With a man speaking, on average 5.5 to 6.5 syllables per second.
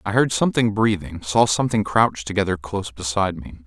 Yes: male; 6.3 syllables/s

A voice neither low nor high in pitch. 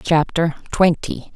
Yes: medium, 165 Hz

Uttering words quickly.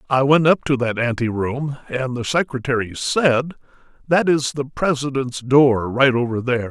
No: average, 160 wpm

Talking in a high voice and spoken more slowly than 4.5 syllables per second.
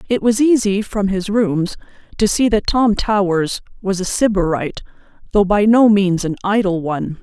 No: high, 200 Hz; 4.9 syllables/s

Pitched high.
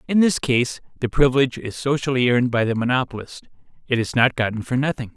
No: low, 125 Hz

